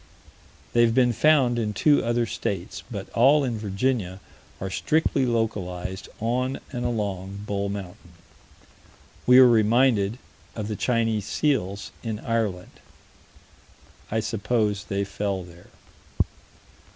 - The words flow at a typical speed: No, slow, 120 wpm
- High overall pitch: No, low, 110 Hz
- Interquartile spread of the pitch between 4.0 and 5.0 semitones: No, average, 3.5 semitones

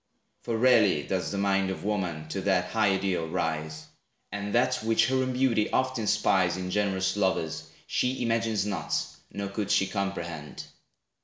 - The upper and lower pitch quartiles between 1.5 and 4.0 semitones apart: Yes, average, 3.1 semitones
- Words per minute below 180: Yes, average, 160 wpm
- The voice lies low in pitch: Yes, low, 100 Hz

